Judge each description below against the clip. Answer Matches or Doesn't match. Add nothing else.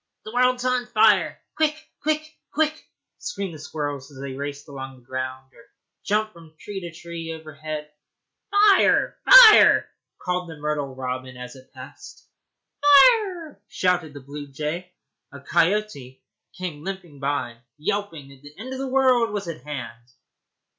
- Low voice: Doesn't match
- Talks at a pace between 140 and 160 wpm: Matches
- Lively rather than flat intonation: Matches